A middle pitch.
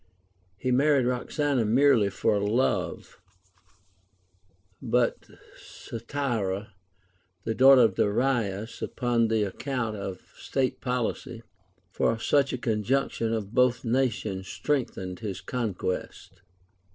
No: low, 115 Hz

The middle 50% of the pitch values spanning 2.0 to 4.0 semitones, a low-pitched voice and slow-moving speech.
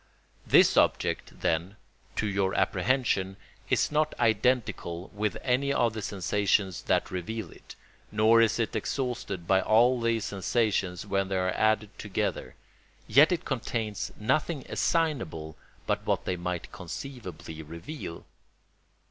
No: average, 4.7 semitones; low, 105 Hz; slow, 130 wpm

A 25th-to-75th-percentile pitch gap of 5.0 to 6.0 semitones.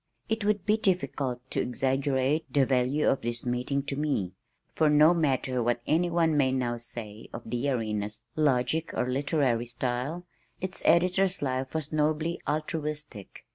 No: average, 4.2 semitones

